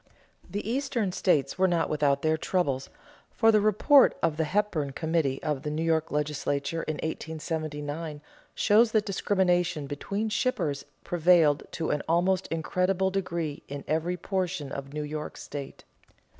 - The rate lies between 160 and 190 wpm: No, average, 145 wpm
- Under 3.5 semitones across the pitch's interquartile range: No, average, 4.2 semitones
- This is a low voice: No, medium, 165 Hz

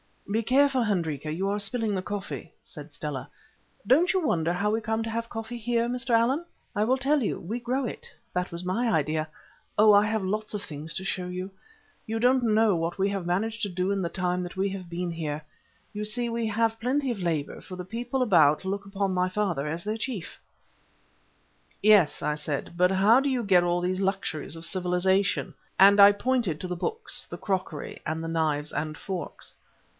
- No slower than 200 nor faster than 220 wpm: Yes, fast, 205 wpm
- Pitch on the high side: Yes, high, 195 Hz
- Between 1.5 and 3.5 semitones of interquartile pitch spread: No, average, 4.3 semitones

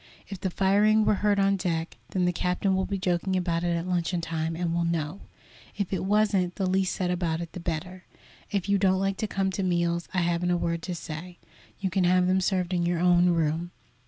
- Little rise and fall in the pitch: Yes, narrow, 2.0 semitones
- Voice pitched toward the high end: No, medium, 180 Hz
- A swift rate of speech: Yes, fast, 230 wpm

